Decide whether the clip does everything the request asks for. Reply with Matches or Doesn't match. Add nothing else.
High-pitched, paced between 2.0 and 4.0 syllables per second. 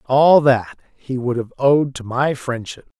Doesn't match